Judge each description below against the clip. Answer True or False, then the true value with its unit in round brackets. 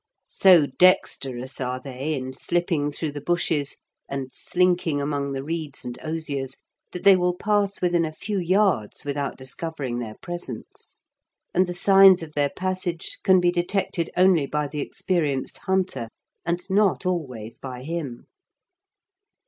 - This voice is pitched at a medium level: True (160 Hz)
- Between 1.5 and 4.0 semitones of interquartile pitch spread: False (4.8 semitones)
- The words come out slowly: False (145 wpm)